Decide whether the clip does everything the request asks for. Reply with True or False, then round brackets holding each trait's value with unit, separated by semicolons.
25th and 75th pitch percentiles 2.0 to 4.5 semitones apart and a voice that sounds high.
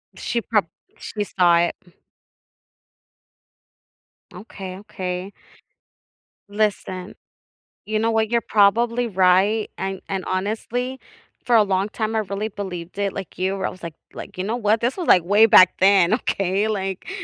True (2.8 semitones; 200 Hz)